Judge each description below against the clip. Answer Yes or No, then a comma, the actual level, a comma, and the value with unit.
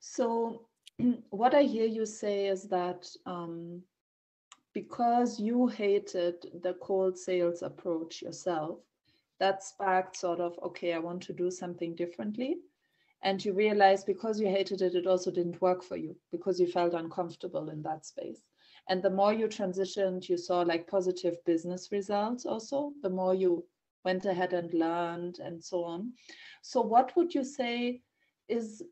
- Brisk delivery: No, average, 160 wpm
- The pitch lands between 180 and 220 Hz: Yes, high, 190 Hz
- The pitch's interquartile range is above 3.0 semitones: Yes, average, 3.9 semitones